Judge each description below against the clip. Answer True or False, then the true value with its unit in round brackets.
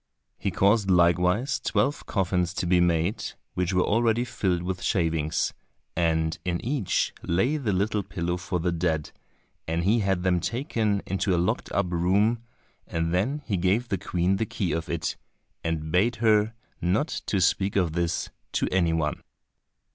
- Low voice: True (90 Hz)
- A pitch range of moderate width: True (3.4 semitones)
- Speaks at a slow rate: False (165 wpm)